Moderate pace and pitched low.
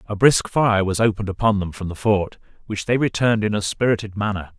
No: fast, 220 wpm; low, 105 Hz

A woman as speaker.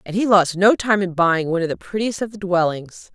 Yes: female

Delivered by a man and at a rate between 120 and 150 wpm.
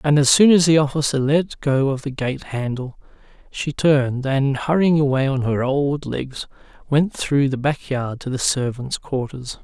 No: male; average, 185 wpm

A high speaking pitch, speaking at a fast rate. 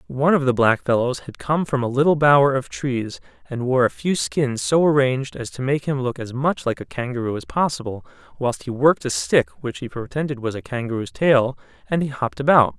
No: low, 130 Hz; fast, 215 wpm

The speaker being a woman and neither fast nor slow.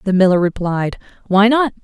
Yes: female; average, 165 wpm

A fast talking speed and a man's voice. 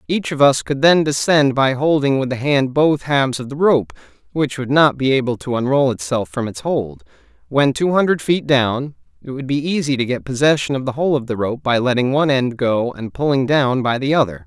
Yes: fast, 230 wpm; male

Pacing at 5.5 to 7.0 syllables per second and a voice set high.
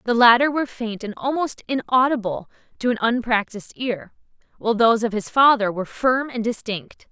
Yes: 5.6 syllables/s; high, 230 Hz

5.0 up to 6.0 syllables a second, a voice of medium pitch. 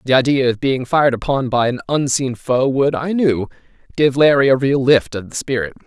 No: 5.4 syllables/s; low, 130 Hz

